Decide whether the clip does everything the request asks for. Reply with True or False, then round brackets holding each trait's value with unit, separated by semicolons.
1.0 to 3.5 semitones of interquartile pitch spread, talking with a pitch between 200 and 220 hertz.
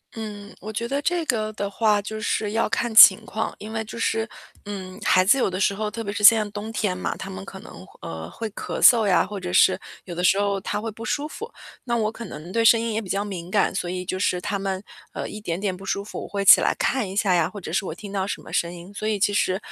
True (2.8 semitones; 205 Hz)